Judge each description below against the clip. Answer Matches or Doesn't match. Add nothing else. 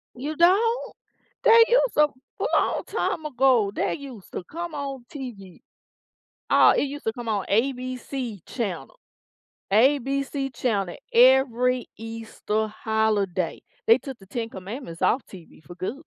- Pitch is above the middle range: Matches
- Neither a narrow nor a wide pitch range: Matches